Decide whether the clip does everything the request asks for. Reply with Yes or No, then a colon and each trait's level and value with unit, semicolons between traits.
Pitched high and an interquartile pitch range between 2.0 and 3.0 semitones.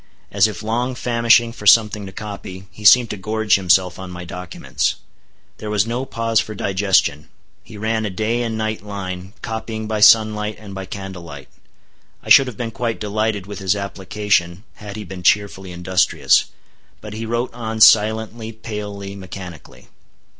No: low, 105 Hz; narrow, 2.5 semitones